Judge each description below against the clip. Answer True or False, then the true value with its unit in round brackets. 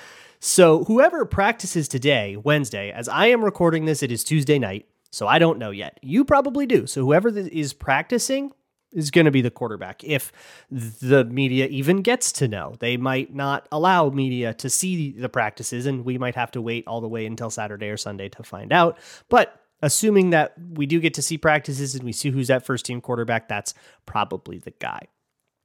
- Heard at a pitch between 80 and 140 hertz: True (135 Hz)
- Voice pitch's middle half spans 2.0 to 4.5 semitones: False (5.6 semitones)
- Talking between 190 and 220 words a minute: True (200 wpm)